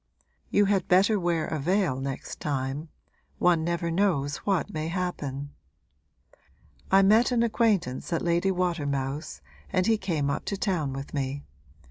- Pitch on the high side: No, medium, 170 Hz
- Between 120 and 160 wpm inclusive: Yes, average, 145 wpm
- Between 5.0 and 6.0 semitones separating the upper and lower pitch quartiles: Yes, average, 5.3 semitones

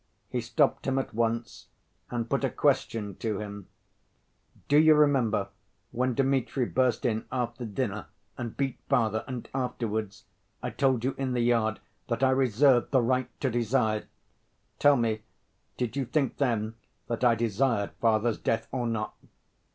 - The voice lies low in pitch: Yes, low, 120 Hz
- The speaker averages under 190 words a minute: Yes, average, 155 wpm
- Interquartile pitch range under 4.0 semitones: Yes, average, 2.9 semitones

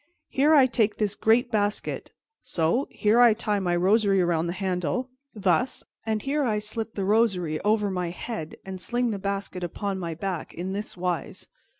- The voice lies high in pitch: Yes, high, 200 Hz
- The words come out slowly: No, average, 180 wpm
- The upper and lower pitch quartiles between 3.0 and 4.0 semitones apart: Yes, average, 3.7 semitones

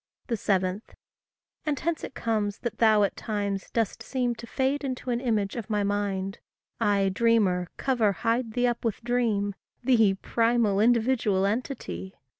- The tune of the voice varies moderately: Yes, average, 3.2 semitones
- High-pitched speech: Yes, high, 220 Hz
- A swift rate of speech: No, average, 150 wpm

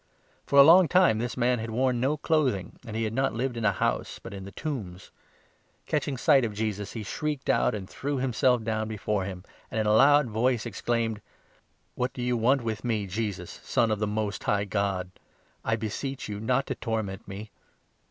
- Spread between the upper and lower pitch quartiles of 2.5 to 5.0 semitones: Yes, average, 3.7 semitones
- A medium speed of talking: No, fast, 210 wpm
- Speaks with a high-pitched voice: No, low, 115 Hz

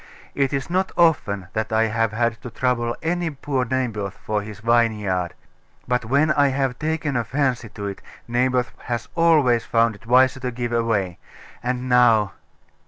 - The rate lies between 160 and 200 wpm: Yes, average, 170 wpm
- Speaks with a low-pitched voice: Yes, low, 120 Hz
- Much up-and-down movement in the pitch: No, average, 3.2 semitones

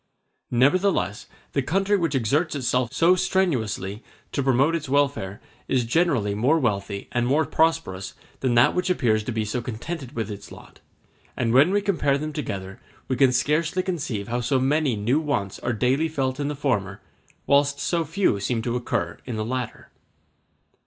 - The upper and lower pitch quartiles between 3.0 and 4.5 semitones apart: No, wide, 5.5 semitones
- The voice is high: No, low, 130 Hz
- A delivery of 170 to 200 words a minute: Yes, average, 175 wpm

